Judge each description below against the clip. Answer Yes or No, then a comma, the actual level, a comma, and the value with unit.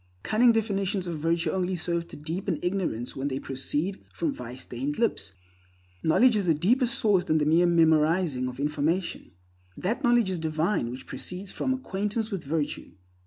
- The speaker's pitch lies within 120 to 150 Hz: No, medium, 175 Hz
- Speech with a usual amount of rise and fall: Yes, average, 4.9 semitones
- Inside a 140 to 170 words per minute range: Yes, average, 165 wpm